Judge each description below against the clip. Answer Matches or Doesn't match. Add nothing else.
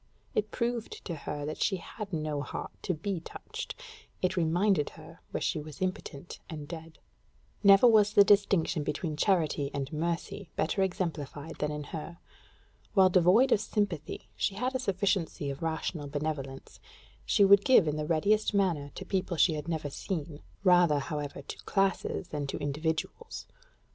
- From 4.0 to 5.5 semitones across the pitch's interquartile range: Matches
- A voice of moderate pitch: Matches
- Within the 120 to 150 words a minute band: Doesn't match